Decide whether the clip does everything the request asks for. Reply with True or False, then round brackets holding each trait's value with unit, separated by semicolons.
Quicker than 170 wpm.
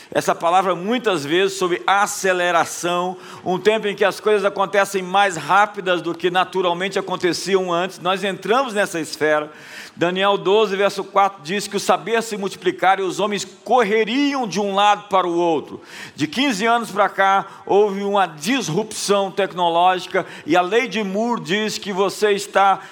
False (160 wpm)